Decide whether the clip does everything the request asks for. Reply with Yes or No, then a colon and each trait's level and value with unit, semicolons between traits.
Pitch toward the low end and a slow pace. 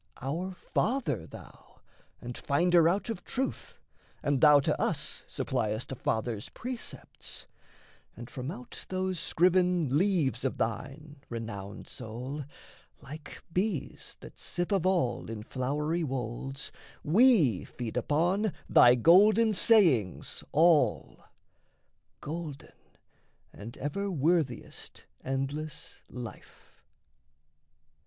No: medium, 150 Hz; slow, 105 wpm